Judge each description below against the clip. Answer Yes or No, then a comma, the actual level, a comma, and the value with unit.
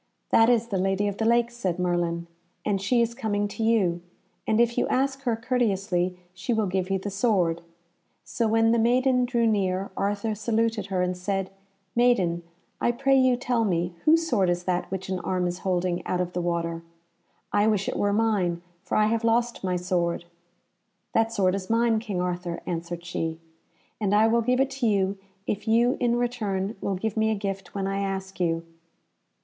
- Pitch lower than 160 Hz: No, high, 200 Hz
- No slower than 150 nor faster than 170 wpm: No, average, 195 wpm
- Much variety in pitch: No, average, 4.0 semitones